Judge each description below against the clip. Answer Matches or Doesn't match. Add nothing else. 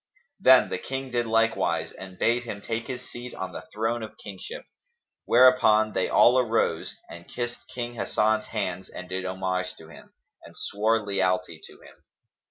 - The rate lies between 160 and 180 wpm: Matches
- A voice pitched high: Doesn't match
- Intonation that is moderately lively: Matches